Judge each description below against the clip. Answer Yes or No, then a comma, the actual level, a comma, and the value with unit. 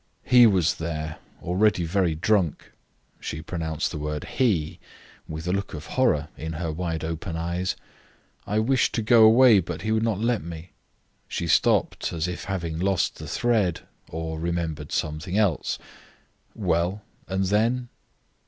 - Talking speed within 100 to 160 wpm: Yes, average, 155 wpm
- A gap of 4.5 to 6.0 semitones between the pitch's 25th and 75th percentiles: Yes, average, 4.8 semitones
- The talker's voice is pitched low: Yes, very low, 90 Hz